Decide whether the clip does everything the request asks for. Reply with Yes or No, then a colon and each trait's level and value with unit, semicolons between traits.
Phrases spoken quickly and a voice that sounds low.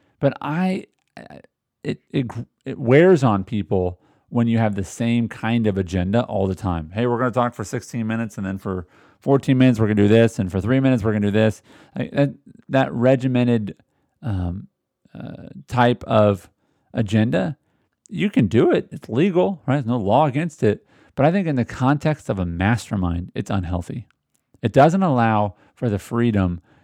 No: average, 185 wpm; low, 115 Hz